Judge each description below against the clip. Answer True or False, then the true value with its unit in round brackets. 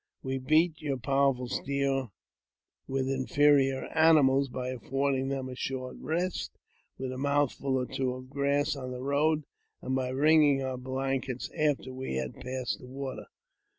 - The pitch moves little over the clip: True (1.6 semitones)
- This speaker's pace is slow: False (150 wpm)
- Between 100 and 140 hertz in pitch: True (135 Hz)